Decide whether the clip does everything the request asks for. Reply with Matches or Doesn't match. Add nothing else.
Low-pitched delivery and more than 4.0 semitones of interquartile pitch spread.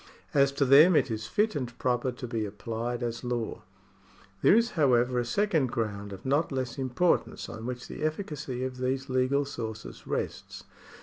Doesn't match